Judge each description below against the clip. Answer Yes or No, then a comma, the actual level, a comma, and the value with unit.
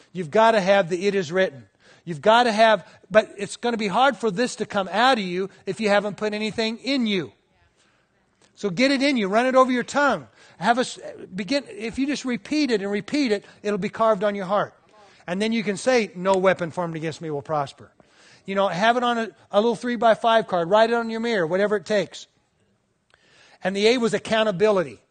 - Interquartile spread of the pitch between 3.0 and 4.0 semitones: Yes, average, 3.3 semitones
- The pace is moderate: No, fast, 230 wpm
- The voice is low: No, high, 210 Hz